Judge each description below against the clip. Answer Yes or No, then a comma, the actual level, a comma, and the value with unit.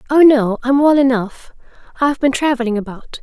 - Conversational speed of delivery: Yes, average, 165 wpm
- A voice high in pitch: Yes, very high, 260 Hz